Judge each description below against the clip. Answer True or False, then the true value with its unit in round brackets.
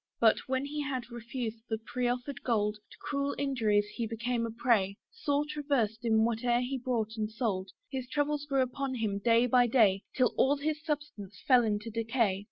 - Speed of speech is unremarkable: True (180 wpm)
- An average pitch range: True (3.6 semitones)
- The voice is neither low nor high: False (240 Hz)